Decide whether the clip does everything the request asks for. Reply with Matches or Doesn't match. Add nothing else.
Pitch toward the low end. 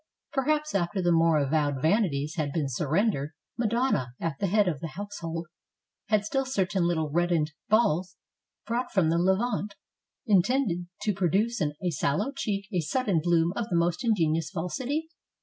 Doesn't match